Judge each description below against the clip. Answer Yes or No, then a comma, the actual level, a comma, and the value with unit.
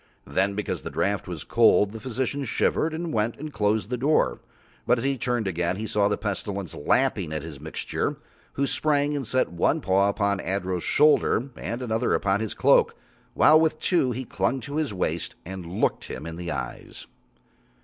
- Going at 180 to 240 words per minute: Yes, average, 190 wpm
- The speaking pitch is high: No, low, 110 Hz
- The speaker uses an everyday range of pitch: No, wide, 5.8 semitones